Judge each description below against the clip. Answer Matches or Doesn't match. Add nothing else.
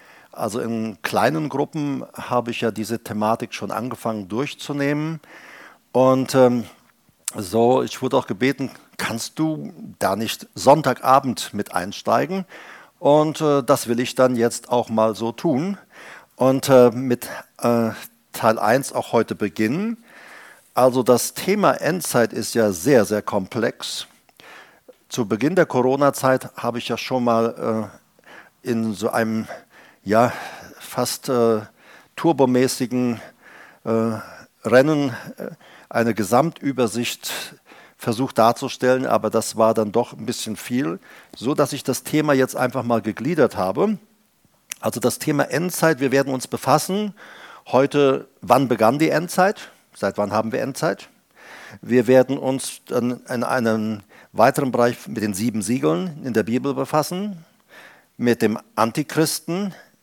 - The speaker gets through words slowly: Doesn't match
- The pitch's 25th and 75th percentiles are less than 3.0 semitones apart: Doesn't match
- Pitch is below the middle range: Matches